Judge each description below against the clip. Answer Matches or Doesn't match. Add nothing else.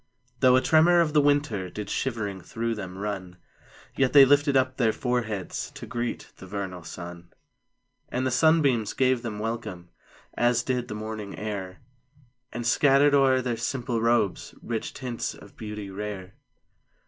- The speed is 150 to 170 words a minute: Matches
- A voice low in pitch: Matches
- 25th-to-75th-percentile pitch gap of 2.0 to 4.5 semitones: Matches